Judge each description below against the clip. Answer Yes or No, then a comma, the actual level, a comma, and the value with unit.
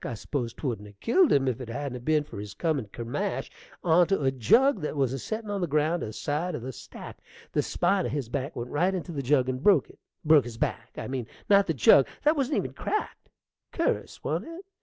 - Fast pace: Yes, fast, 230 wpm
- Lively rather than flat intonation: Yes, wide, 6.4 semitones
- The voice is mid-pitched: Yes, medium, 145 Hz